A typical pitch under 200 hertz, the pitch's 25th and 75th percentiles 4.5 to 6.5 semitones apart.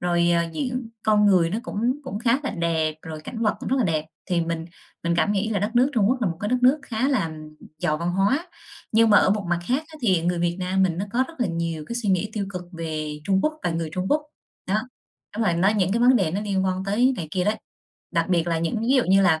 Yes: high, 190 Hz; average, 5.2 semitones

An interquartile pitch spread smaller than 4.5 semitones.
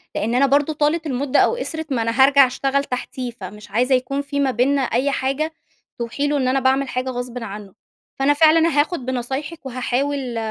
Yes: narrow, 2.4 semitones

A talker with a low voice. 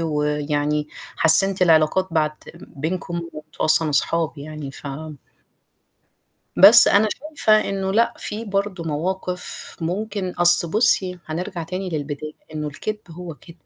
No: medium, 170 Hz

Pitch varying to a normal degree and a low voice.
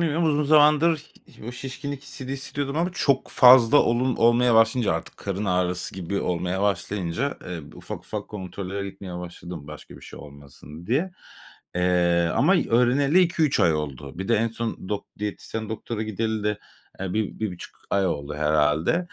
No: wide, 6.9 semitones; low, 105 Hz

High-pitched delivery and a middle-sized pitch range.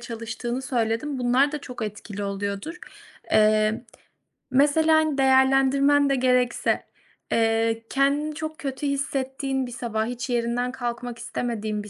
Yes: very high, 250 Hz; average, 3.3 semitones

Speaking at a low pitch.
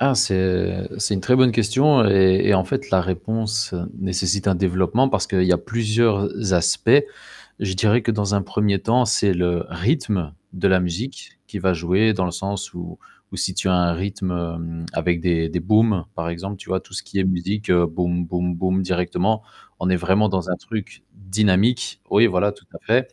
Yes: very low, 95 Hz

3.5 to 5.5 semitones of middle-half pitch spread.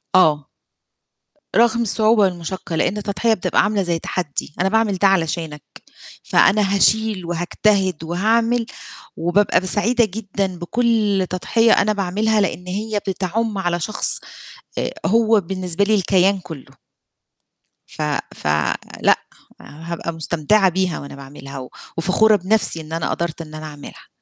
Yes: average, 4.0 semitones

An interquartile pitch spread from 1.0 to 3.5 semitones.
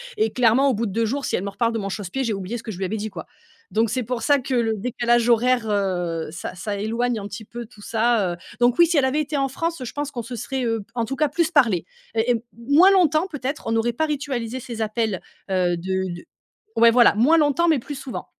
No: average, 4.2 semitones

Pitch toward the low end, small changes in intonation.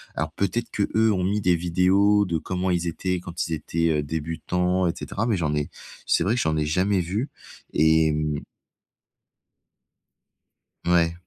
No: very low, 90 Hz; average, 3.1 semitones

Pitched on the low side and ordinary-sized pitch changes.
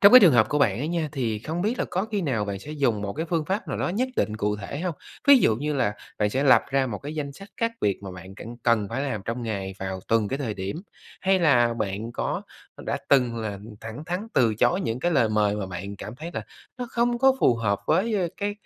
No: low, 125 Hz; wide, 8.4 semitones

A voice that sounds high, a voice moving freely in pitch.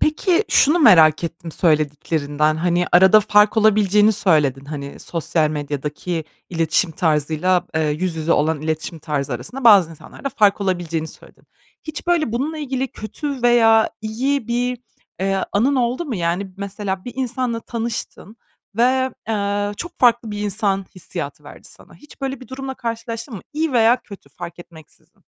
Yes: high, 205 Hz; wide, 6.8 semitones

